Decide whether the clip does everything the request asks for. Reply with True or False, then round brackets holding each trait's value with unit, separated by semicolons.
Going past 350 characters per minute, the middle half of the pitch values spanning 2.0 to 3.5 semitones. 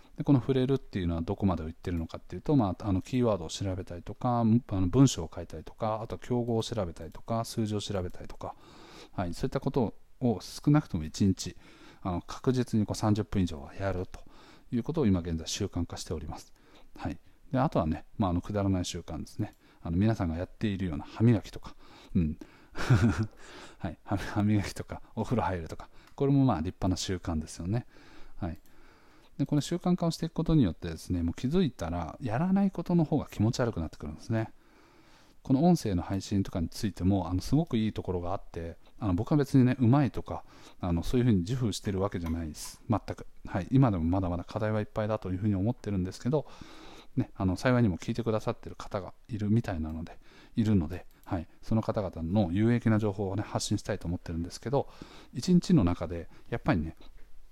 False (430 characters per minute; 5.2 semitones)